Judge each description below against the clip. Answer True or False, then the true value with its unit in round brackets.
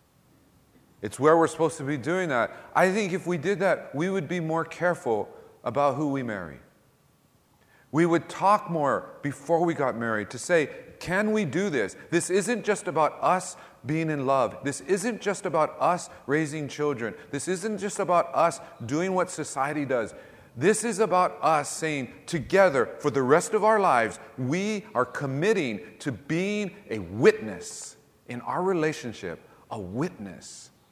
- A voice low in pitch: False (165 Hz)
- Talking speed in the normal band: True (165 wpm)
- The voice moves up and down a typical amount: True (4.8 semitones)